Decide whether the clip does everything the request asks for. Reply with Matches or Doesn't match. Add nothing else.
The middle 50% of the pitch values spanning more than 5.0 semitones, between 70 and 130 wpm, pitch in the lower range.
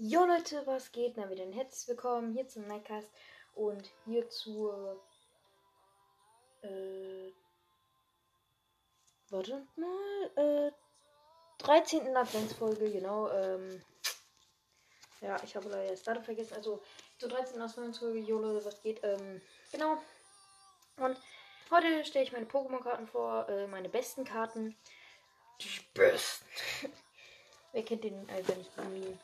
Doesn't match